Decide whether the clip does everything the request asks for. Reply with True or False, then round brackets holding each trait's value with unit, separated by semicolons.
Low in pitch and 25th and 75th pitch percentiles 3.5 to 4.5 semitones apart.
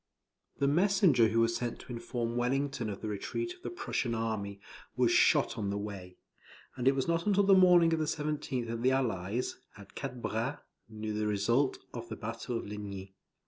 False (120 Hz; 5.0 semitones)